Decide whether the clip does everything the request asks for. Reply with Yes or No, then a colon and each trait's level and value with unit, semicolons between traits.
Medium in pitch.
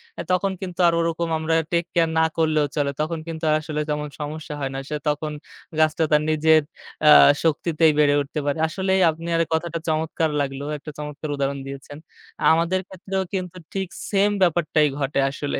Yes: medium, 160 Hz